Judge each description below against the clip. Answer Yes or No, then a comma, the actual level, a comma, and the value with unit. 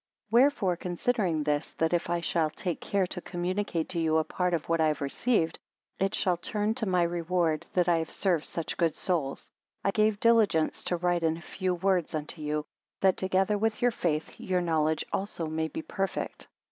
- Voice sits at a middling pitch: Yes, medium, 175 Hz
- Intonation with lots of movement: No, average, 3.1 semitones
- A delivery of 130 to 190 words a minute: No, average, 200 wpm